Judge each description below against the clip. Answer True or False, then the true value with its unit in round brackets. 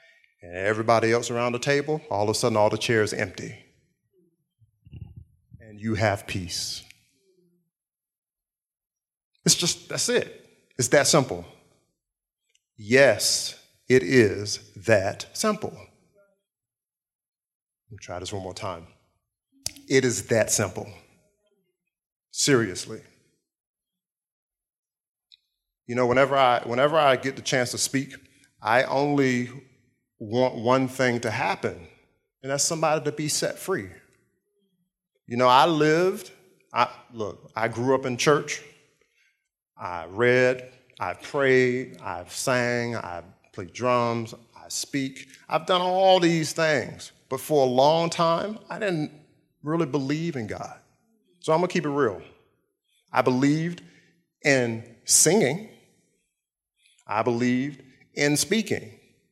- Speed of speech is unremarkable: False (120 wpm)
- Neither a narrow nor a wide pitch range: False (5.7 semitones)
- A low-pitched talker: True (130 Hz)